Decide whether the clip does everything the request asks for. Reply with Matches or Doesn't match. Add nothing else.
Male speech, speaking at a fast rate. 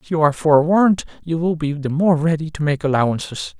Matches